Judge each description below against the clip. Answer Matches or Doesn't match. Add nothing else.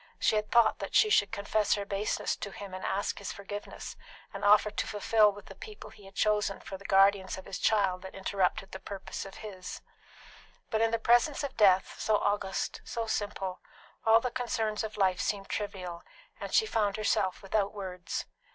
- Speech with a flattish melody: Matches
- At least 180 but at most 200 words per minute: Matches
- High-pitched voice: Matches